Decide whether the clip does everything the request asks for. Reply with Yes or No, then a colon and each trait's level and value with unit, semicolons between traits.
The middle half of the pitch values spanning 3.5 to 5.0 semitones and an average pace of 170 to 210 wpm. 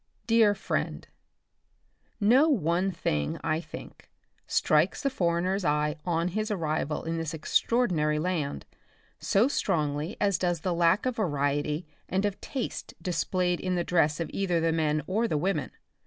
No: average, 4.3 semitones; average, 155 wpm